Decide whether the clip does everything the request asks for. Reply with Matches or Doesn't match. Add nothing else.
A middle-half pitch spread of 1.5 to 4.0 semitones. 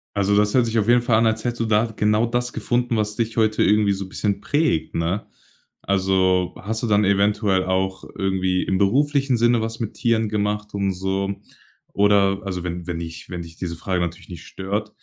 Matches